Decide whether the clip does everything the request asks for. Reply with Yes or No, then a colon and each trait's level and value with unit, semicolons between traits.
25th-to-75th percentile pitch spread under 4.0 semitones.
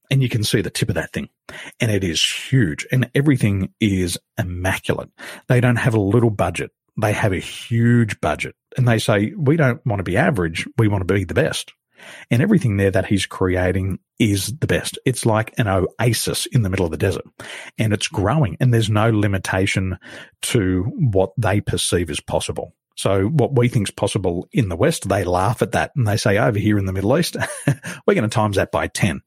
No: average, 4.4 semitones